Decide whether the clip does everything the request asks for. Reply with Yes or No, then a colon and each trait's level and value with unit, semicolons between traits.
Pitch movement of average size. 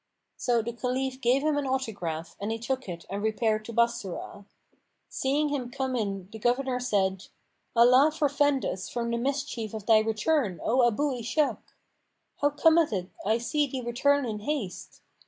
Yes: average, 4.1 semitones